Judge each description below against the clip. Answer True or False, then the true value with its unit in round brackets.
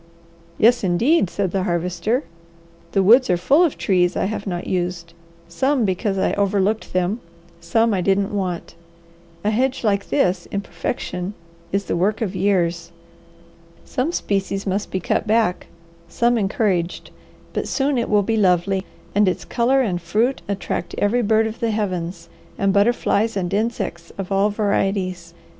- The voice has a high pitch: True (200 Hz)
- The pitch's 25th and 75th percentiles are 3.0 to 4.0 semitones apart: True (3.5 semitones)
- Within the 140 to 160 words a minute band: True (155 wpm)